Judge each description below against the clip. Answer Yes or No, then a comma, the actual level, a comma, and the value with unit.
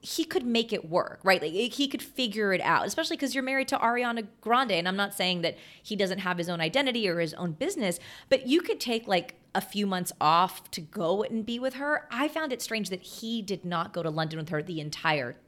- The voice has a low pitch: No, high, 205 Hz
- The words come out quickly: Yes, fast, 250 wpm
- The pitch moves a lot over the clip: Yes, wide, 6.2 semitones